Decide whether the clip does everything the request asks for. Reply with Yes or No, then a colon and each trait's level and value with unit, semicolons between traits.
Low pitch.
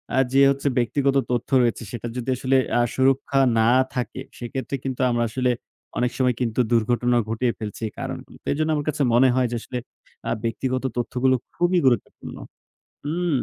Yes: low, 125 Hz